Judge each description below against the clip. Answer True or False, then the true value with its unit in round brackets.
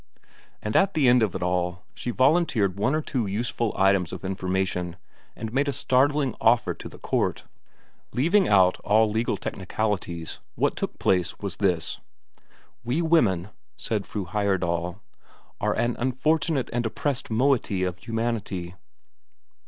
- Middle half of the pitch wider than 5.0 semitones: True (5.5 semitones)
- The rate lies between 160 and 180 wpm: False (145 wpm)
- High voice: False (110 Hz)